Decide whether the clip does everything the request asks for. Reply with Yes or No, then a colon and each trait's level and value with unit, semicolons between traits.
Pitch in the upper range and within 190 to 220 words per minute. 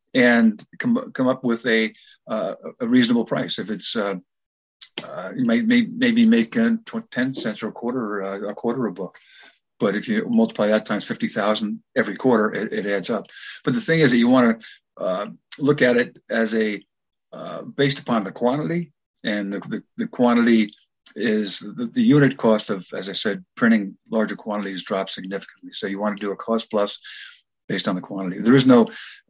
No: low, 120 Hz; average, 200 wpm